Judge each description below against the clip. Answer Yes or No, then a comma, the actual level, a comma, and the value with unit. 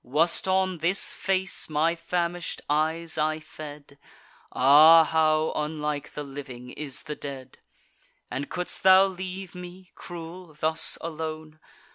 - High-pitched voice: No, medium, 160 Hz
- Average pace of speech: No, slow, 125 wpm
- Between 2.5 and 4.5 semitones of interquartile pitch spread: Yes, average, 2.9 semitones